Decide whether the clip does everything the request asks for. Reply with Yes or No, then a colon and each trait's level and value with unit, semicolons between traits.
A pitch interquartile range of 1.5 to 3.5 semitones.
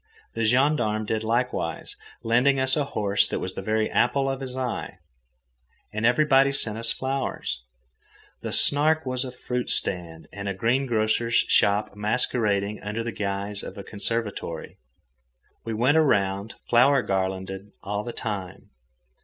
No: average, 4.0 semitones